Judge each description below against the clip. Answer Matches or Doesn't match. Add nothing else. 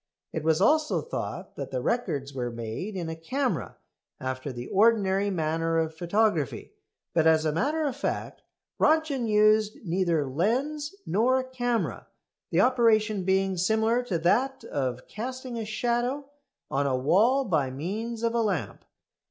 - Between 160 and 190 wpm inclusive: Doesn't match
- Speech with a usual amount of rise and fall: Doesn't match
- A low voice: Doesn't match